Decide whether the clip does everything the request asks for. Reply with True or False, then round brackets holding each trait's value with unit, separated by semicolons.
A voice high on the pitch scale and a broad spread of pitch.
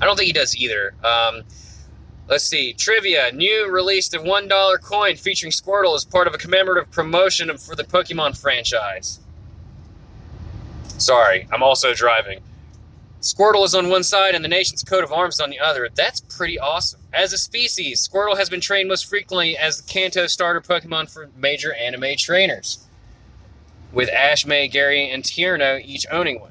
False (160 Hz; 6.8 semitones)